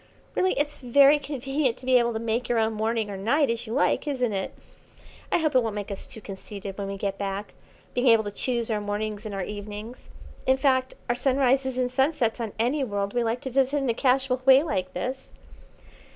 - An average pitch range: Yes, average, 4.0 semitones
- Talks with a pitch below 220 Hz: No, high, 240 Hz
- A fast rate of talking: Yes, fast, 220 wpm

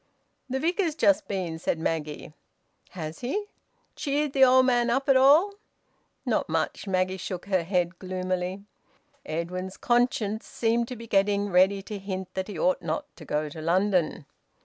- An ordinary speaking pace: Yes, average, 160 wpm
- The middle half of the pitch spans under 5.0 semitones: No, average, 5.3 semitones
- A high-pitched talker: Yes, high, 195 Hz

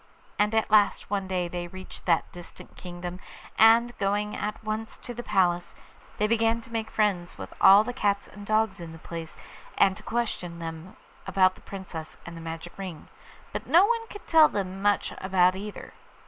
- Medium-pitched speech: No, high, 195 Hz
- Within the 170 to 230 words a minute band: Yes, average, 190 wpm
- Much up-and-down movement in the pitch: No, average, 3.7 semitones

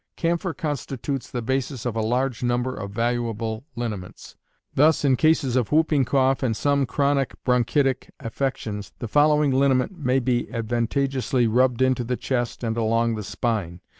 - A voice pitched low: Yes, low, 125 Hz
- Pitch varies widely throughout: No, average, 2.9 semitones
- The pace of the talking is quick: No, average, 155 wpm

